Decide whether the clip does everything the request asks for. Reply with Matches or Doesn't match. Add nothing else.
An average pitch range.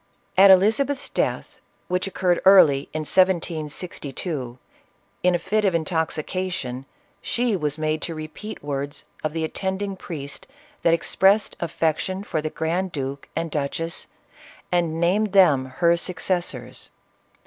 Matches